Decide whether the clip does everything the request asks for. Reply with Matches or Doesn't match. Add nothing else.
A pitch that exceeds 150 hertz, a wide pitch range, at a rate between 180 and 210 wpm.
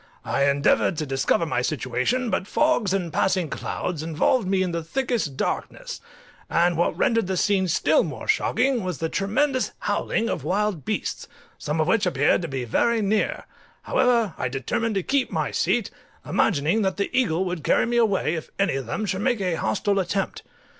Matches